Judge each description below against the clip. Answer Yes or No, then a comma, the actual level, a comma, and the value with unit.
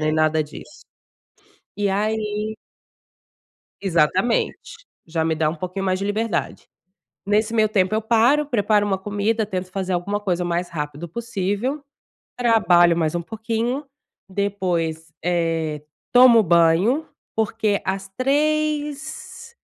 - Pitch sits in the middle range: No, high, 200 Hz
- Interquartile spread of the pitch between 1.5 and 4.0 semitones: No, average, 4.7 semitones